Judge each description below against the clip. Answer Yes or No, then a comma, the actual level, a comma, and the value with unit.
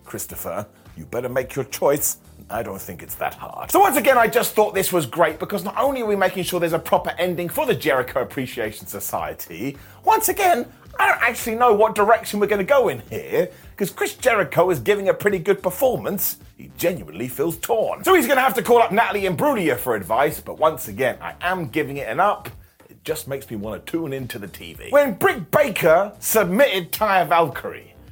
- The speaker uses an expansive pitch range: Yes, wide, 6.1 semitones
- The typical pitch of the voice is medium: No, high, 200 Hz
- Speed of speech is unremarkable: No, fast, 215 wpm